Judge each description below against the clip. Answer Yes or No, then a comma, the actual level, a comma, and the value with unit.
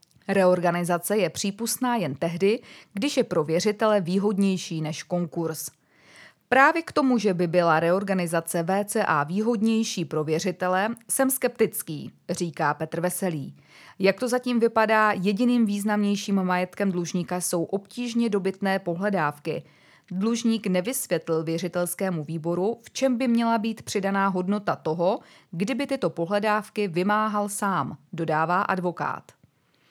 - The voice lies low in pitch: No, high, 195 Hz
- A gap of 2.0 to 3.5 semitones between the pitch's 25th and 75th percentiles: No, average, 4.0 semitones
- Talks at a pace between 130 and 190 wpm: No, average, 120 wpm